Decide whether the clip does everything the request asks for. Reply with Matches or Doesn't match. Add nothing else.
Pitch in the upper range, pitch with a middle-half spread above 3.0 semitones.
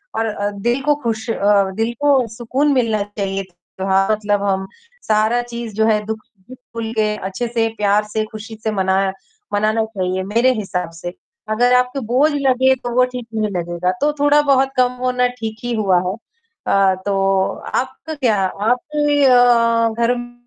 Matches